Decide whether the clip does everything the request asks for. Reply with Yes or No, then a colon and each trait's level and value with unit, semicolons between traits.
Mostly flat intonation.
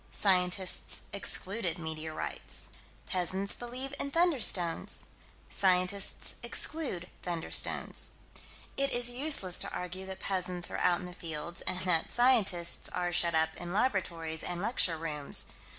No: average, 3.7 semitones